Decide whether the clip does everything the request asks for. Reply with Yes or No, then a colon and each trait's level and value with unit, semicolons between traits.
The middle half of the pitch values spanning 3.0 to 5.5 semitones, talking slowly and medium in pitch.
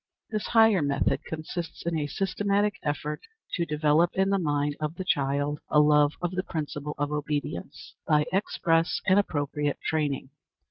No: average, 3.6 semitones; average, 155 wpm; medium, 150 Hz